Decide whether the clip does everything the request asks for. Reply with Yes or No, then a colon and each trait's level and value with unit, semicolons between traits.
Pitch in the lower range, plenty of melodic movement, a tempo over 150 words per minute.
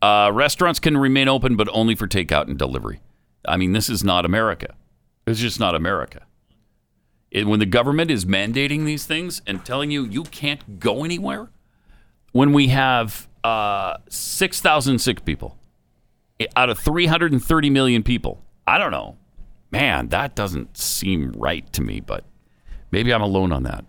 Yes: low, 120 Hz; wide, 5.8 semitones; average, 160 wpm